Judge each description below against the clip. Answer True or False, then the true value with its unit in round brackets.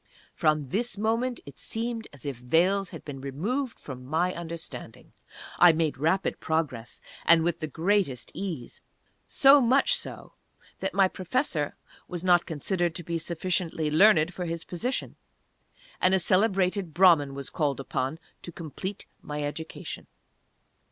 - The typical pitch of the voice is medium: True (170 Hz)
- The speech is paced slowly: False (145 wpm)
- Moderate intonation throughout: True (4.3 semitones)